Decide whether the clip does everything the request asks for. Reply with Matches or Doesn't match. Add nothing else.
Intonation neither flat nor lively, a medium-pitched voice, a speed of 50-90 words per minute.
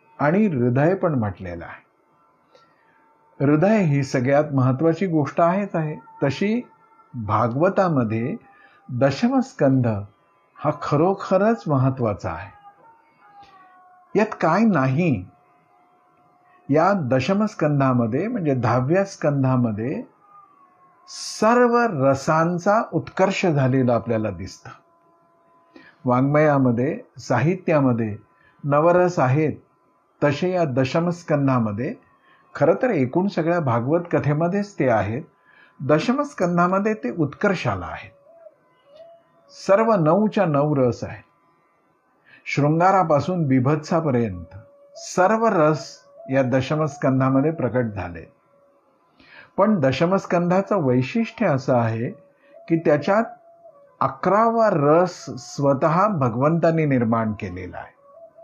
Doesn't match